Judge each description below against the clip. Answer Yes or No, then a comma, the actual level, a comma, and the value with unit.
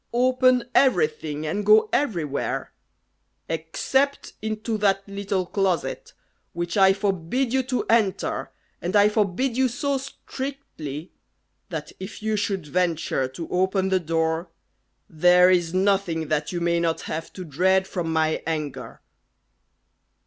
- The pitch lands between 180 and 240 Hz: Yes, high, 190 Hz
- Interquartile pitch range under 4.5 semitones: No, average, 4.8 semitones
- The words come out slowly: Yes, slow, 130 wpm